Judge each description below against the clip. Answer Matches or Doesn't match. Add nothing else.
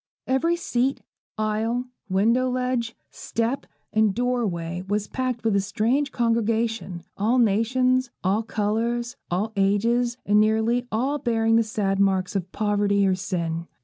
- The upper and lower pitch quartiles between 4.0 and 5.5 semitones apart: Doesn't match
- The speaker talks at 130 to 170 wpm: Matches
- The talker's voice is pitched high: Matches